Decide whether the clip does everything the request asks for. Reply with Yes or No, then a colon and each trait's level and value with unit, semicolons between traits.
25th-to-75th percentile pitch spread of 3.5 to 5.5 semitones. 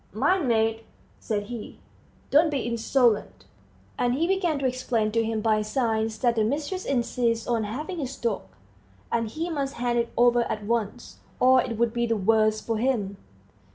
No: average, 3.0 semitones